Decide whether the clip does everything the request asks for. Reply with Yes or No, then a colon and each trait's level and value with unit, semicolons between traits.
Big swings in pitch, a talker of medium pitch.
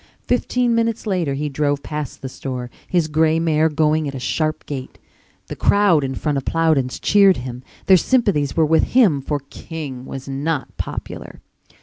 No: average, 3.6 semitones; medium, 155 Hz